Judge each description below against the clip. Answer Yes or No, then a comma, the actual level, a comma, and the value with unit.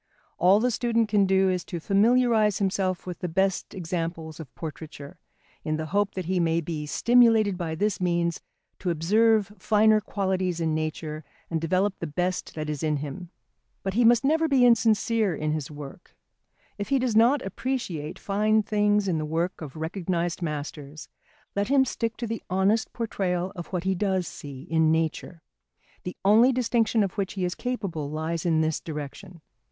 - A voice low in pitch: No, medium, 185 Hz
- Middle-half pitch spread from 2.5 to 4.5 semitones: No, average, 4.9 semitones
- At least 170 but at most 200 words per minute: Yes, average, 180 wpm